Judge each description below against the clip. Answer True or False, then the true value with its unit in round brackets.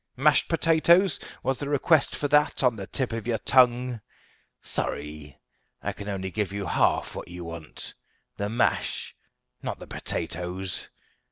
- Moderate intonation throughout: False (7.1 semitones)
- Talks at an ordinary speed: True (150 wpm)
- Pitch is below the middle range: True (115 Hz)